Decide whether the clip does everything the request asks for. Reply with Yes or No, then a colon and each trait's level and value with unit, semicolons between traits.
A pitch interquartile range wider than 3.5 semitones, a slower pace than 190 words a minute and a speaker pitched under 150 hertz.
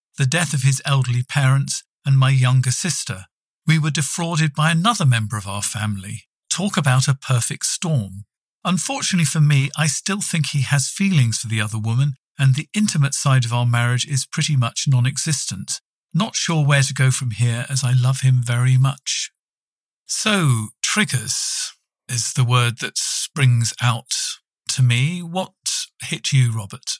Yes: average, 4.3 semitones; average, 170 wpm; low, 135 Hz